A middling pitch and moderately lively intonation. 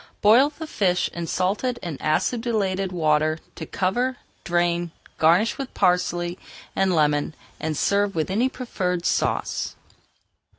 Yes: medium, 180 Hz; average, 4.2 semitones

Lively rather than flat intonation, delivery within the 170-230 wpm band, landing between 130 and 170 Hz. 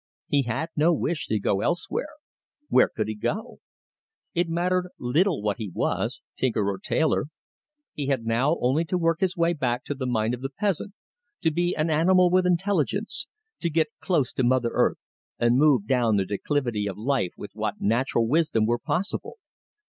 Yes: wide, 6.7 semitones; average, 180 wpm; medium, 140 Hz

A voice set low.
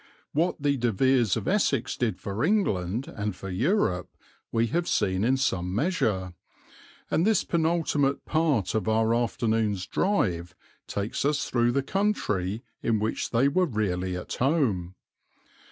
Yes: low, 115 Hz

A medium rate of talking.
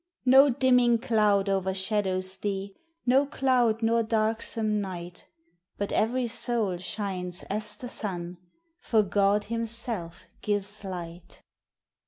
No: slow, 110 wpm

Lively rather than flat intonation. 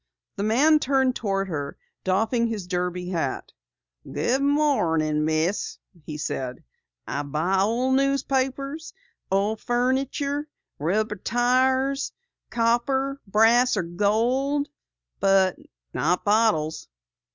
Yes: wide, 6.7 semitones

